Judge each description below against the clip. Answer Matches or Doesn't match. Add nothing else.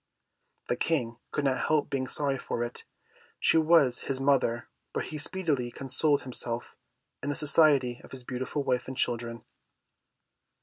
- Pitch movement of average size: Matches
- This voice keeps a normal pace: Matches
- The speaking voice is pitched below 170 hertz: Matches